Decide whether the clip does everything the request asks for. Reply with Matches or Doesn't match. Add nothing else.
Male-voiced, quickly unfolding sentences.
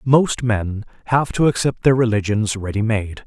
Doesn't match